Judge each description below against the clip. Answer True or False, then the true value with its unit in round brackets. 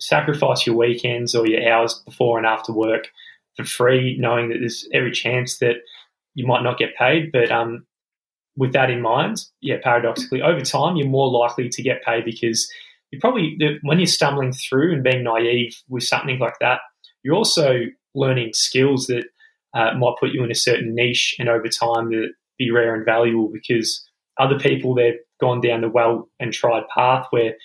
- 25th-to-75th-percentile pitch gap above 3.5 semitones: False (2.5 semitones)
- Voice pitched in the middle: False (120 Hz)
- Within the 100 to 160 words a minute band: False (185 wpm)